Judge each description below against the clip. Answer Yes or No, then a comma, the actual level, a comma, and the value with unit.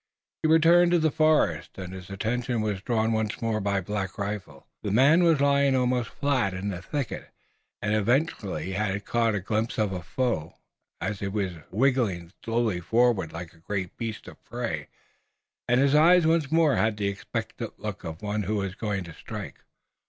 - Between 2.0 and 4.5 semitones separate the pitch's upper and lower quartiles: No, average, 5.2 semitones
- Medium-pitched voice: No, low, 110 Hz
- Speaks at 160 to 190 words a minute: Yes, average, 185 wpm